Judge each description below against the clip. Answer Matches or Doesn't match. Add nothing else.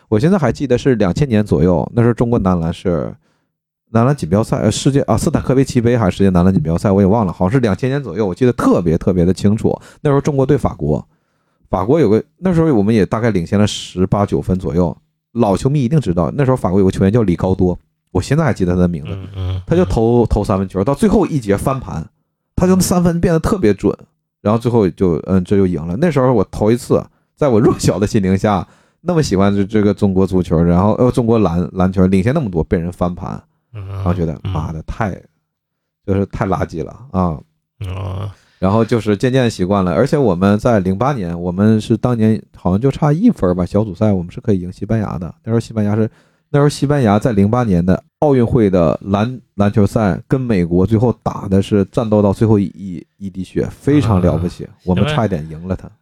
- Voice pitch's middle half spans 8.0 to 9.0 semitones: Doesn't match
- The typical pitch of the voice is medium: Doesn't match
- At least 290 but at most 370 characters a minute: Matches